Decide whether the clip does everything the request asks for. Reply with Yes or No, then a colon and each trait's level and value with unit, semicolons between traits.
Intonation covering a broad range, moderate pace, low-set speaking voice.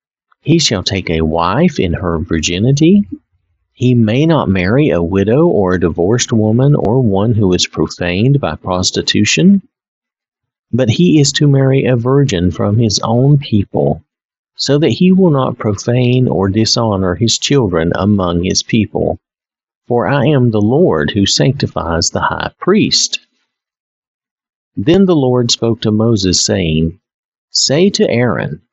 Yes: wide, 6.7 semitones; average, 145 wpm; low, 115 Hz